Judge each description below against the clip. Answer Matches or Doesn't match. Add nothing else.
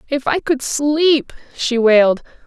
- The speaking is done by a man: Doesn't match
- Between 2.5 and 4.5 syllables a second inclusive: Matches